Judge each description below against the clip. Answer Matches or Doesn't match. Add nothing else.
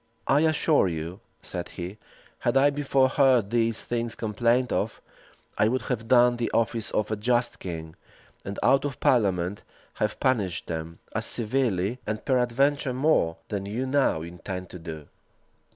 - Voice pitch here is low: Matches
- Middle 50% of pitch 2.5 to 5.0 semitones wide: Doesn't match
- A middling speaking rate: Matches